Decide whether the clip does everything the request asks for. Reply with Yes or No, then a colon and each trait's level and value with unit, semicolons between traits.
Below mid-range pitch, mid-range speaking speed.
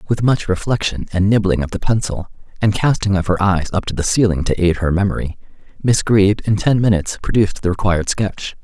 No: low, 100 Hz; fast, 210 wpm